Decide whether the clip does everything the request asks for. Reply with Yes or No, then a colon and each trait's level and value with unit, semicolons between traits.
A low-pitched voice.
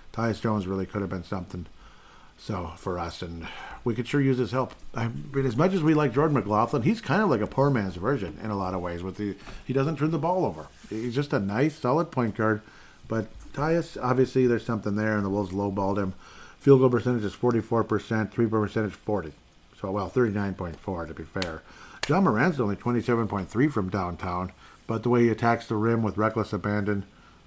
Yes: low, 110 Hz